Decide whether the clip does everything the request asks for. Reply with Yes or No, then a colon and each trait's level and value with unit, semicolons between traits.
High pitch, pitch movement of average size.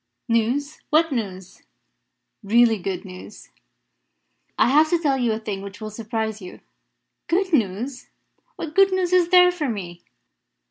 No: high, 235 Hz; wide, 7.4 semitones